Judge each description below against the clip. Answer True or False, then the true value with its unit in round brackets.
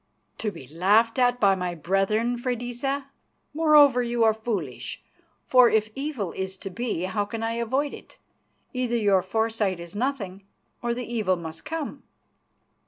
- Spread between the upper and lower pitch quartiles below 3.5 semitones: False (4.2 semitones)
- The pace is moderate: True (155 wpm)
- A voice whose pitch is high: True (225 Hz)